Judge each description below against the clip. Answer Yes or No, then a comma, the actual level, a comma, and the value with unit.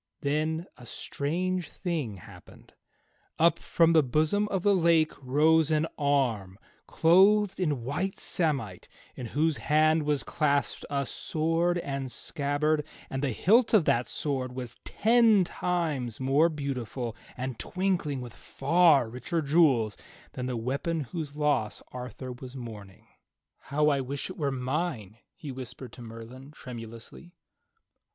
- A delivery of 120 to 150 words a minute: Yes, average, 140 wpm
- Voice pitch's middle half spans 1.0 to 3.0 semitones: No, average, 4.6 semitones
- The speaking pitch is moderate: Yes, medium, 145 Hz